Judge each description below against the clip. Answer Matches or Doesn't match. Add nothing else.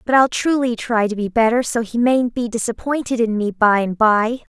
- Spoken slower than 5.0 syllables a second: Doesn't match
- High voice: Matches